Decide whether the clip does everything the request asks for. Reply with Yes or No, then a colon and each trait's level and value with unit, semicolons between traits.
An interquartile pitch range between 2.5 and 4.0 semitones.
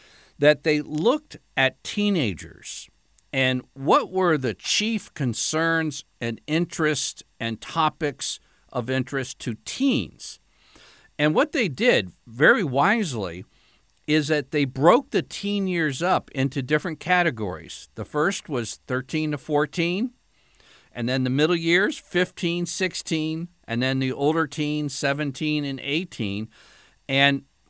No: average, 4.5 semitones